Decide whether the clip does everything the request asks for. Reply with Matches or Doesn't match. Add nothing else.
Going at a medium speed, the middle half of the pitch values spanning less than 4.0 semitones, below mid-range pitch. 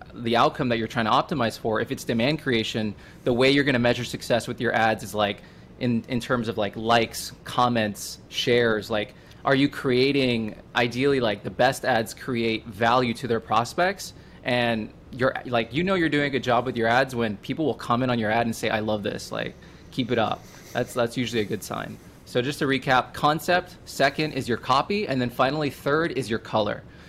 Doesn't match